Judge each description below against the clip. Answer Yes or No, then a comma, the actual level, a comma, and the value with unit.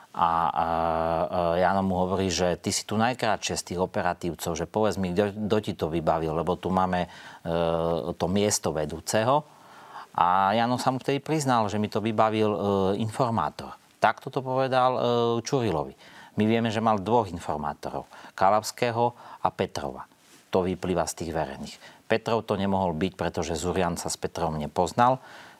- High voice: No, very low, 95 Hz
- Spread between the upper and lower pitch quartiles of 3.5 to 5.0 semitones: Yes, average, 4.6 semitones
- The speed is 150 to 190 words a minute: Yes, average, 160 wpm